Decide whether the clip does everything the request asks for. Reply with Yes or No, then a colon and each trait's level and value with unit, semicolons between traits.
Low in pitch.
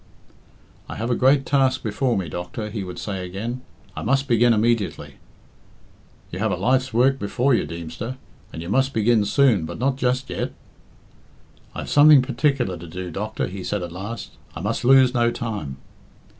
Yes: low, 115 Hz